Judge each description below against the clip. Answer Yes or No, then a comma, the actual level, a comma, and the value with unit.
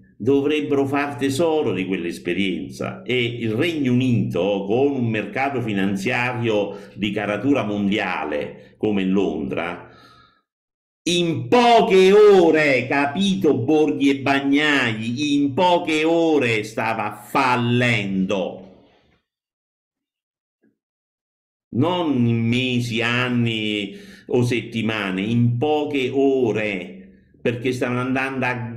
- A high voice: No, low, 125 Hz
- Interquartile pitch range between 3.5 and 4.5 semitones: No, average, 4.9 semitones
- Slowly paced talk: Yes, slow, 90 wpm